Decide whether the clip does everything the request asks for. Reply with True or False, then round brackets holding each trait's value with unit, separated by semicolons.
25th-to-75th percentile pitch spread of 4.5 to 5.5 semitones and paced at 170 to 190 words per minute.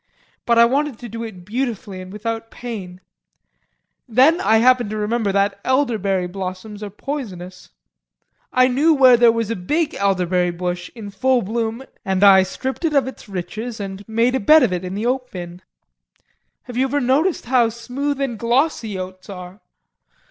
True (4.8 semitones; 175 wpm)